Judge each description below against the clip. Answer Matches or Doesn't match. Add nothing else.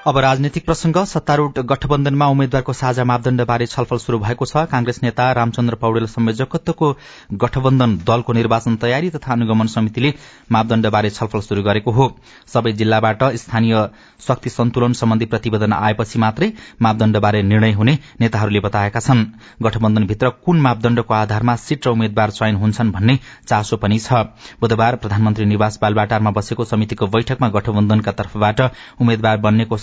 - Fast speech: Doesn't match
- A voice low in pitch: Matches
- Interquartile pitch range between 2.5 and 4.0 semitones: Matches